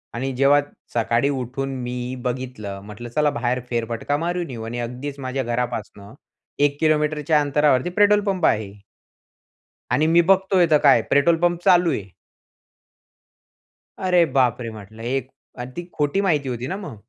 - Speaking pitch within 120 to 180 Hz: Yes, low, 135 Hz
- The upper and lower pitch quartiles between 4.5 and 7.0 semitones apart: Yes, average, 5.1 semitones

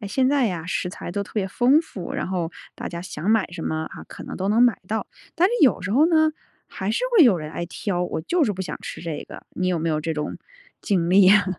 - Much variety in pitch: Yes, wide, 5.7 semitones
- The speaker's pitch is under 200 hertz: Yes, high, 190 Hz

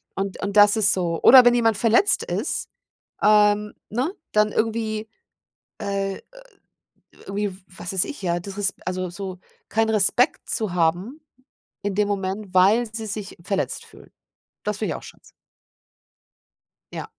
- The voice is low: No, high, 205 Hz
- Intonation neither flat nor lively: No, narrow, 2.3 semitones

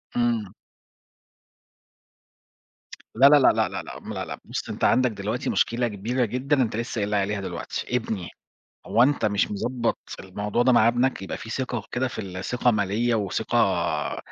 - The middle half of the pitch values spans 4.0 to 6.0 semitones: No, average, 3.3 semitones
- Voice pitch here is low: Yes, low, 115 Hz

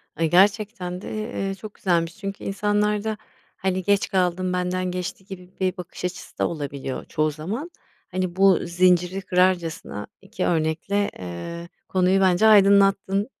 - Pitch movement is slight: Yes, narrow, 2.3 semitones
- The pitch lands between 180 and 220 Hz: Yes, medium, 185 Hz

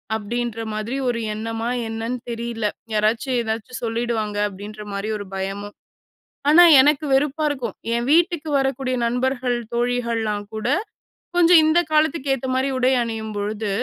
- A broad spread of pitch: No, average, 3.6 semitones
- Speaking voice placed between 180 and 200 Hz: No, high, 235 Hz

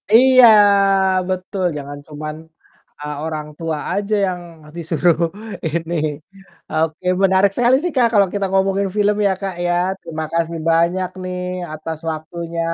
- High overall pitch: No, medium, 175 Hz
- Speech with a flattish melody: No, average, 3.4 semitones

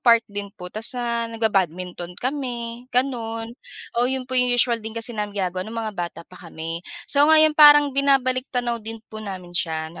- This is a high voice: Yes, high, 230 Hz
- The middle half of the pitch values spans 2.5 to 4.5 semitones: No, average, 4.9 semitones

